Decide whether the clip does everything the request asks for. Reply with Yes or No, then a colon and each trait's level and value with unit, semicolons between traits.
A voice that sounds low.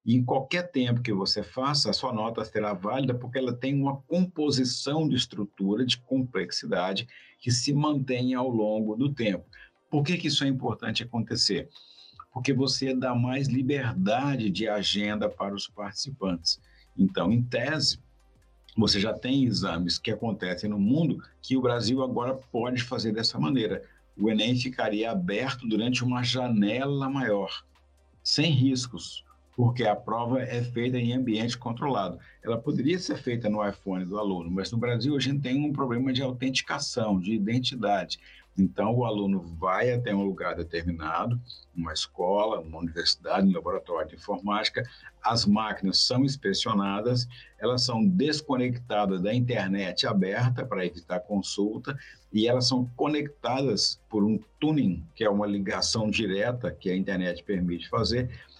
Yes: low, 120 Hz